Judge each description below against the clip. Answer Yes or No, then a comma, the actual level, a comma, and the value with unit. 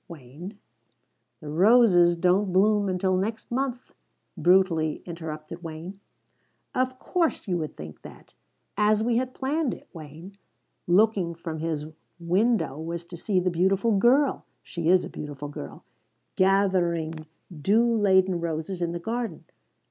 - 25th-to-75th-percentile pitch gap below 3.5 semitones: No, average, 4.4 semitones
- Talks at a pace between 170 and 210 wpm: No, average, 140 wpm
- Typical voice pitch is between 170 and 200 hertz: Yes, medium, 185 Hz